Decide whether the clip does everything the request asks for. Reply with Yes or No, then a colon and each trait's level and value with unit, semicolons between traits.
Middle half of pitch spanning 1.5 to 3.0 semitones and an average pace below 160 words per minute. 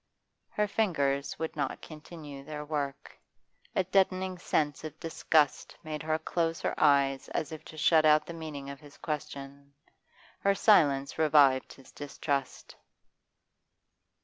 Yes: narrow, 2.6 semitones; slow, 135 wpm